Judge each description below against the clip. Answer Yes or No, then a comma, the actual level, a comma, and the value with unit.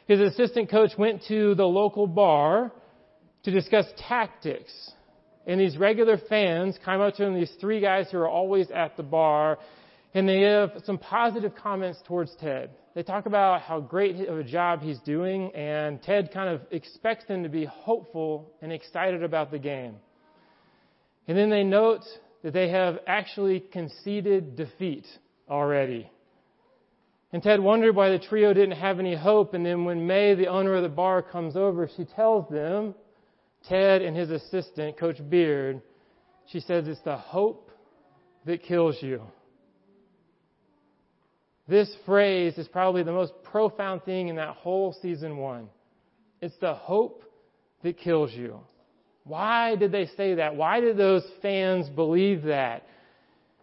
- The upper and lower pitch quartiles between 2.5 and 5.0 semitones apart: Yes, average, 3.7 semitones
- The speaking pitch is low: No, medium, 185 Hz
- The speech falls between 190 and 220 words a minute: No, average, 155 wpm